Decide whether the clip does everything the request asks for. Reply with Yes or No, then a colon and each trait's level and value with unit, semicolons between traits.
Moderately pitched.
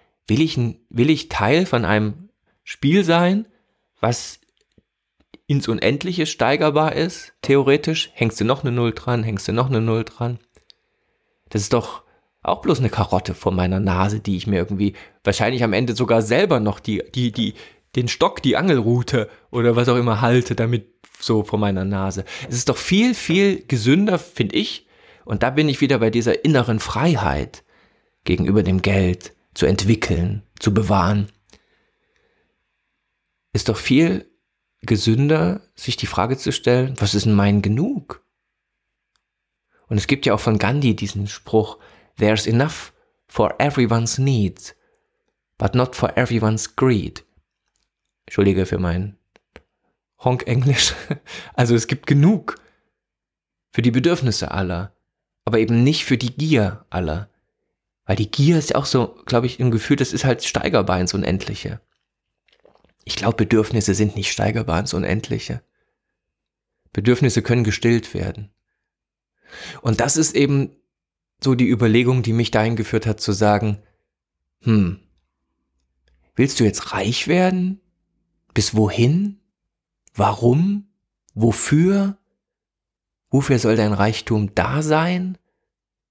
No: low, 115 Hz